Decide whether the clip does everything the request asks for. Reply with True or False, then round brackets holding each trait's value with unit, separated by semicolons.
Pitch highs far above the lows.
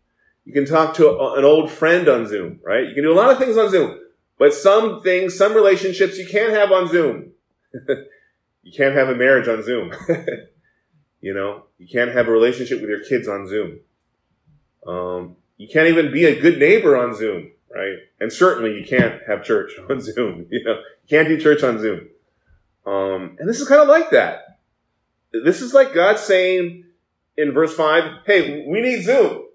True (8.9 semitones)